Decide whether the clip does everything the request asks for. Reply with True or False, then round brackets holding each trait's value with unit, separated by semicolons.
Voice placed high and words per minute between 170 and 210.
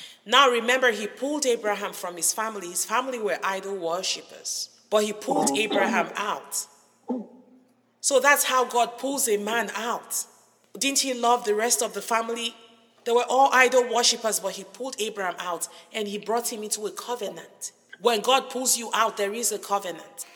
True (230 Hz; 175 wpm)